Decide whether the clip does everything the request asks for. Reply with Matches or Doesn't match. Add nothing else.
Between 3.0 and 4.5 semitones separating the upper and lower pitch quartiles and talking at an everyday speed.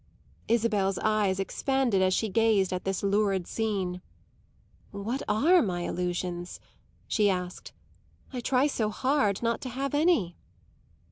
Doesn't match